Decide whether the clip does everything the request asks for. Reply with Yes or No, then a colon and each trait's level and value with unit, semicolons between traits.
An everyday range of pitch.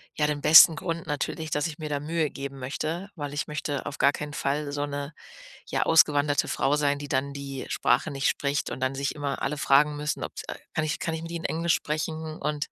No: narrow, 1.8 semitones